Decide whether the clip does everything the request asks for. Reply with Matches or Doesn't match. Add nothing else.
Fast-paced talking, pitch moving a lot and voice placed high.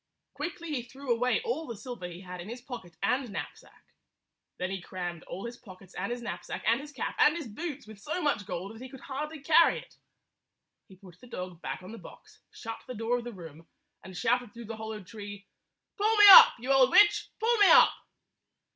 Matches